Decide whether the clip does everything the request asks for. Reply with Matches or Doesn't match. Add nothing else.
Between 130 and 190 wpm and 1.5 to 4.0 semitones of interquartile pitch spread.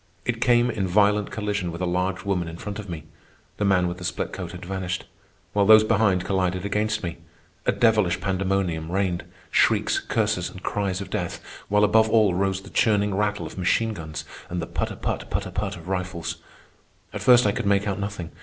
Doesn't match